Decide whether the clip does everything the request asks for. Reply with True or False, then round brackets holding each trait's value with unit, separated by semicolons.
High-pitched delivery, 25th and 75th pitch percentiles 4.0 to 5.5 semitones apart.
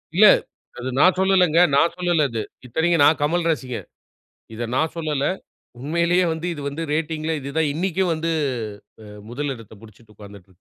False (155 Hz; 4.6 semitones)